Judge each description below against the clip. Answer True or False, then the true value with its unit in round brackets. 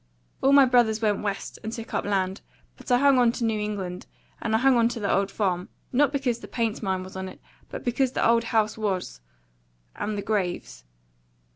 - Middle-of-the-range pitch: False (220 Hz)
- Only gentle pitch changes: False (3.7 semitones)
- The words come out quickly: True (215 wpm)